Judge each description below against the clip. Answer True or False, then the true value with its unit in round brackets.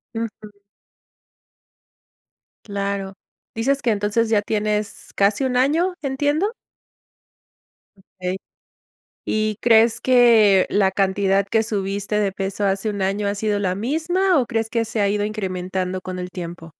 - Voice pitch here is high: True (210 Hz)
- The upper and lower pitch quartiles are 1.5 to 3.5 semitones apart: True (2.9 semitones)